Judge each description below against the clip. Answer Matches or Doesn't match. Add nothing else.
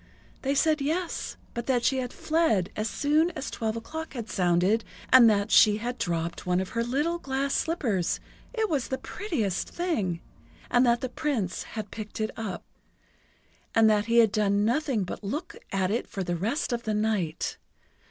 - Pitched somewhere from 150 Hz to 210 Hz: Doesn't match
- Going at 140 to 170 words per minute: Doesn't match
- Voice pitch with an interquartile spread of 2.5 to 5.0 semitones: Doesn't match